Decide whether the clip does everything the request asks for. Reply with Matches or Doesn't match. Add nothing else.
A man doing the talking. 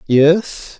Matches